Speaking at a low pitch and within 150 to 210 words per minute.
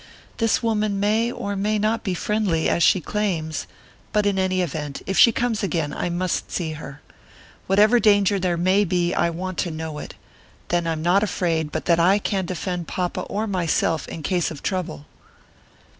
No: medium, 185 Hz; average, 185 wpm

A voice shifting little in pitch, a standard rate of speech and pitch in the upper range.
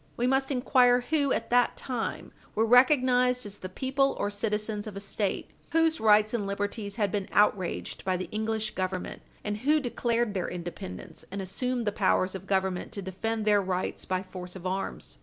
No: average, 4.4 semitones; average, 185 wpm; high, 210 Hz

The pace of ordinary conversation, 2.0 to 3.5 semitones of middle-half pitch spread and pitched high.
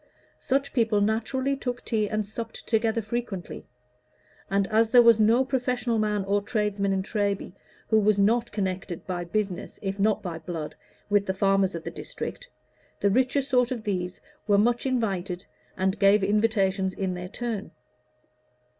Yes: average, 160 wpm; average, 3.2 semitones; high, 210 Hz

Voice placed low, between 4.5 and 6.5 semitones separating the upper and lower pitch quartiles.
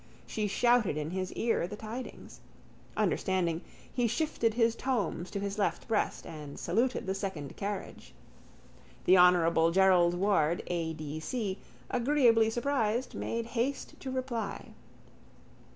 No: high, 205 Hz; average, 5.0 semitones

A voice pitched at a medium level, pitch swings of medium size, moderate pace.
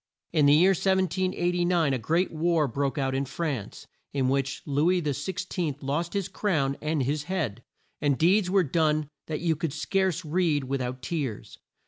Yes: medium, 155 Hz; average, 4.3 semitones; average, 175 wpm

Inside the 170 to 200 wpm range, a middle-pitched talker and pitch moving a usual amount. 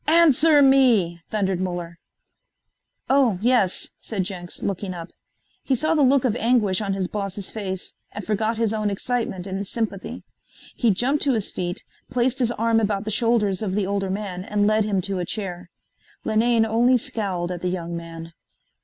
No: average, 175 wpm; high, 205 Hz; average, 4.0 semitones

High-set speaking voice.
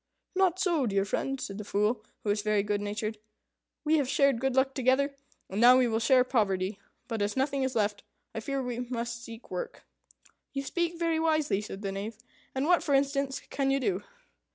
Yes: very high, 250 Hz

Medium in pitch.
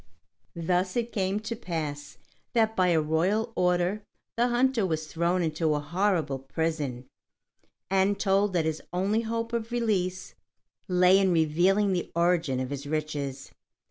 Yes: medium, 180 Hz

